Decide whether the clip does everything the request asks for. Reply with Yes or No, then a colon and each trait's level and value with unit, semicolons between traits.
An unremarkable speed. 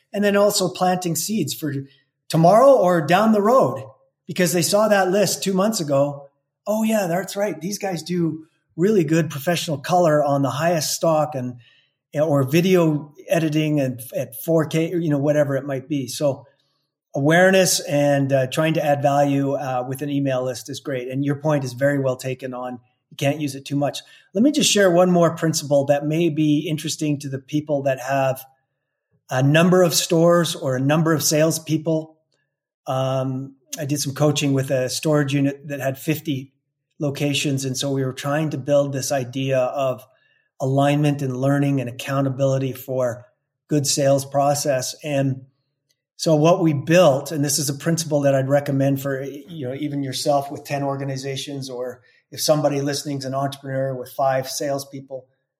Yes: average, 180 wpm